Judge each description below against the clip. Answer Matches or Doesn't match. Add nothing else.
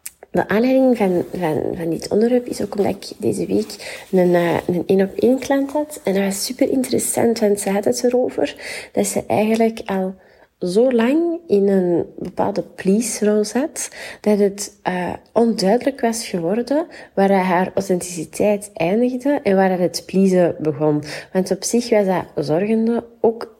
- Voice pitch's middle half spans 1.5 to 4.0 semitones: Doesn't match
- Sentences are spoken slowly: Doesn't match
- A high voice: Matches